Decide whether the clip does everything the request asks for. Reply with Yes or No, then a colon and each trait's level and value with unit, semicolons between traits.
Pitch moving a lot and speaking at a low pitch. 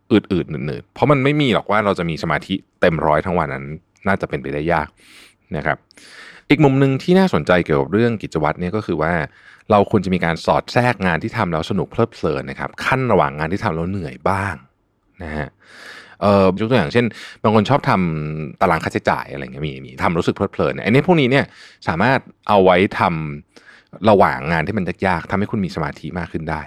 Yes: wide, 5.7 semitones; very low, 95 Hz